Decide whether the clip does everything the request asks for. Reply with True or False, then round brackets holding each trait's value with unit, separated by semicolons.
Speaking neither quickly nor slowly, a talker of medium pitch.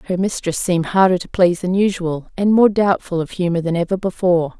False (210 wpm; 180 Hz)